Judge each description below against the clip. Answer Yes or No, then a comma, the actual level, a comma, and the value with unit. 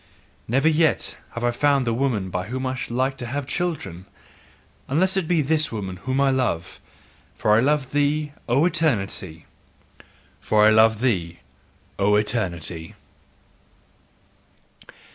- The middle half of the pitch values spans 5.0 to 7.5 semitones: Yes, wide, 5.6 semitones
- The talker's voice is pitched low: Yes, low, 125 Hz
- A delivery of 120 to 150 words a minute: Yes, average, 140 wpm